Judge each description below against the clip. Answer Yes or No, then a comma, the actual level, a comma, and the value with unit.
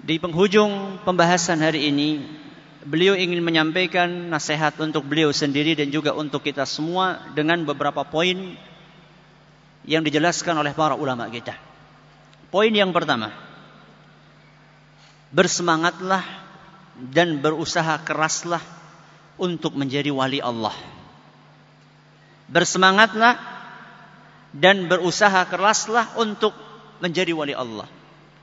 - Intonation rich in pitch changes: No, average, 3.3 semitones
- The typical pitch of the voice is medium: Yes, medium, 160 Hz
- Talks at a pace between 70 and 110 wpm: Yes, average, 95 wpm